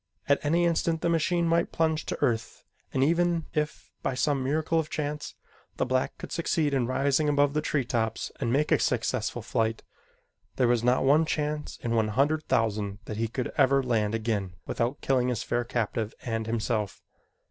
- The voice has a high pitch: No, low, 135 Hz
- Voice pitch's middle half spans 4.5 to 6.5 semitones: Yes, average, 4.8 semitones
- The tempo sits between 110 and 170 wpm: No, average, 185 wpm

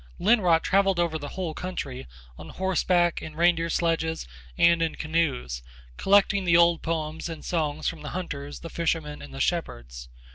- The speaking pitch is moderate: Yes, medium, 165 Hz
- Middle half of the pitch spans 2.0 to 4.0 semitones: Yes, narrow, 2.6 semitones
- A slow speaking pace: No, average, 160 wpm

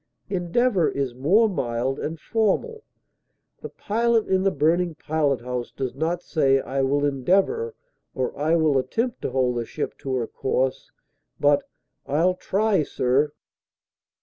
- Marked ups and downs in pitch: Yes, wide, 6.2 semitones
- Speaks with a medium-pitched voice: Yes, medium, 155 Hz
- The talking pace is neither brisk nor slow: Yes, average, 145 wpm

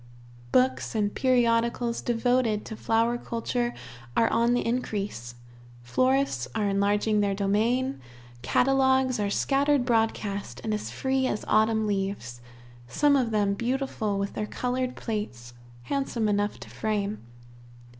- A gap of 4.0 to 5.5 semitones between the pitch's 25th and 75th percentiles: No, average, 3.6 semitones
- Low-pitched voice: No, high, 220 Hz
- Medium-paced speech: No, slow, 125 wpm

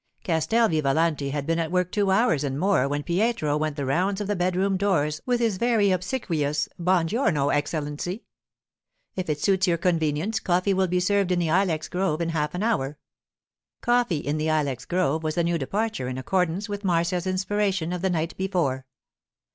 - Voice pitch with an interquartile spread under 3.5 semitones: No, average, 4.1 semitones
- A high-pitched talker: No, medium, 175 Hz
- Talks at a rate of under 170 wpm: No, average, 185 wpm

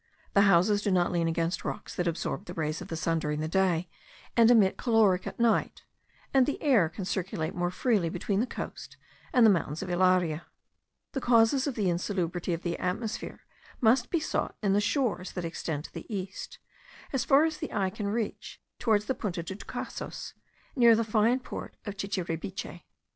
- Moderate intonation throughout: Yes, average, 4.6 semitones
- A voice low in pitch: No, high, 195 Hz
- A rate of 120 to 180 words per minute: No, average, 190 wpm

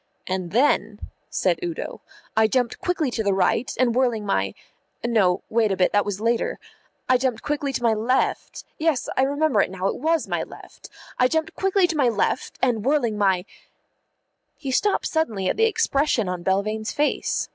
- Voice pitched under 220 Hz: No, high, 240 Hz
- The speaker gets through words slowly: No, average, 185 wpm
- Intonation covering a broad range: Yes, wide, 6.0 semitones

